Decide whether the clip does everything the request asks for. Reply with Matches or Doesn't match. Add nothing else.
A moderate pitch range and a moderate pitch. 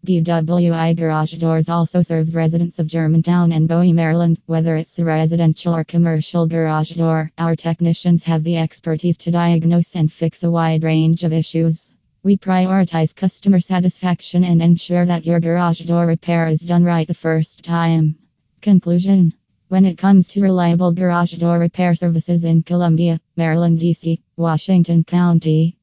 Doesn't match